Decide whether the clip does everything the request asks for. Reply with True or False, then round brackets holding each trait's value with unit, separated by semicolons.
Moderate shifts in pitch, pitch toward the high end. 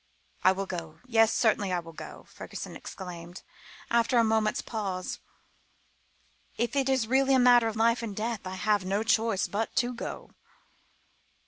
True (3.8 semitones; 220 Hz)